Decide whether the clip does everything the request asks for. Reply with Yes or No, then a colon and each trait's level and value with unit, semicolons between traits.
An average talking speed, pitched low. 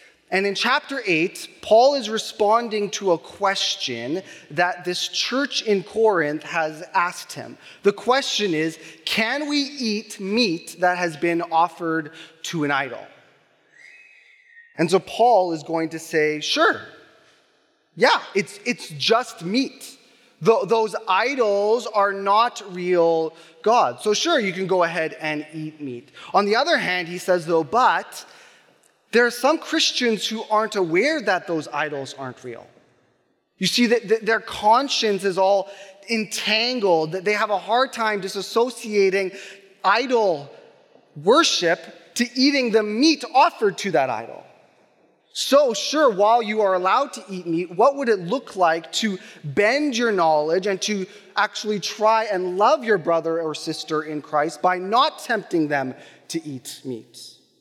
No: average, 150 wpm; high, 200 Hz